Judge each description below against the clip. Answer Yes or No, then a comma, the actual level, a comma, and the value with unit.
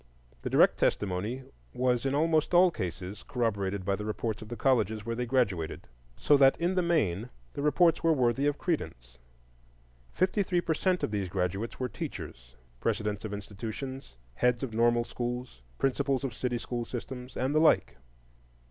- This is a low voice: Yes, low, 120 Hz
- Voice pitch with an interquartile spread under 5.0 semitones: No, average, 5.3 semitones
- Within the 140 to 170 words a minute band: Yes, average, 165 wpm